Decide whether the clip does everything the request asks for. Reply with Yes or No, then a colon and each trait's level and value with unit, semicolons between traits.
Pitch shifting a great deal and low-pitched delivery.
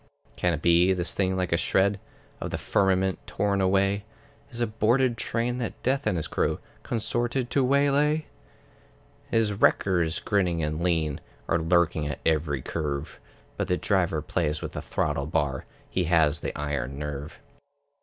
Yes: wide, 5.9 semitones; very low, 90 Hz